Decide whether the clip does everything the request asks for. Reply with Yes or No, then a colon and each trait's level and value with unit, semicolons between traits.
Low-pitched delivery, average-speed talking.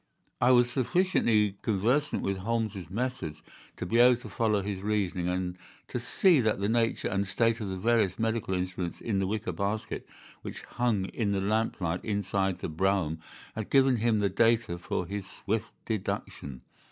Yes: low, 105 Hz; average, 170 wpm